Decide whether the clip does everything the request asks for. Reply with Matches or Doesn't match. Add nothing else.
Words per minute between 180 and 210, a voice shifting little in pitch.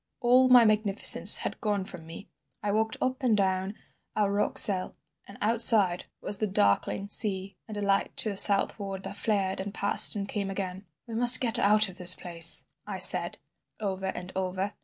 Matches